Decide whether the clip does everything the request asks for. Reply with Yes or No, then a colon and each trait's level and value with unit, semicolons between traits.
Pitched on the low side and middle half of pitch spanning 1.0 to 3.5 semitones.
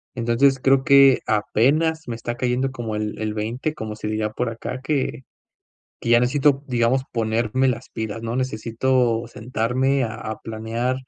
Yes: low, 120 Hz; average, 2.9 semitones